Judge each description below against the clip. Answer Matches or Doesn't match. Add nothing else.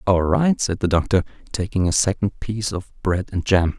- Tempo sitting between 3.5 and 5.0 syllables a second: Doesn't match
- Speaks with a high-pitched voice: Doesn't match